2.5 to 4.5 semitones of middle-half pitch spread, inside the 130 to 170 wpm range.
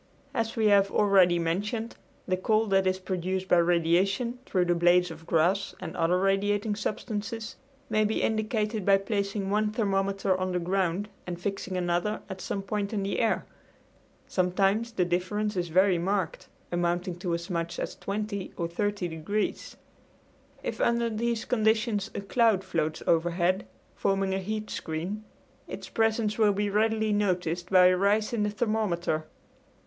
Yes: average, 3.1 semitones; average, 160 wpm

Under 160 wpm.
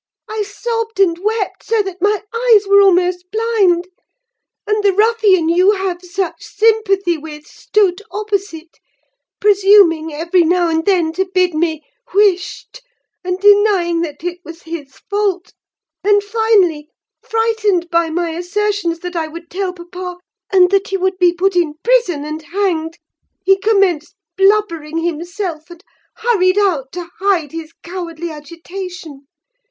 Yes: average, 140 wpm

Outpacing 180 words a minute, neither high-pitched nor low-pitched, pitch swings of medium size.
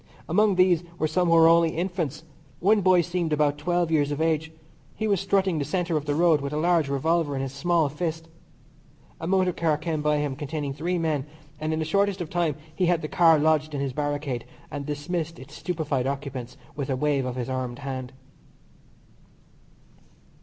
Yes: average, 195 wpm; medium, 155 Hz; average, 3.2 semitones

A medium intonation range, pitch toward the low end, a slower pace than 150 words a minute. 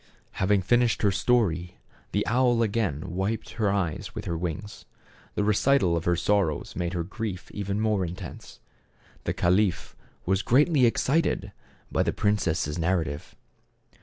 Yes: average, 4.2 semitones; low, 100 Hz; average, 140 wpm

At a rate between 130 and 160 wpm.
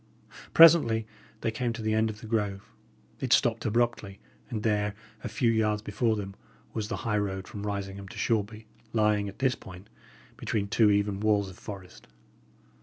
No: average, 175 wpm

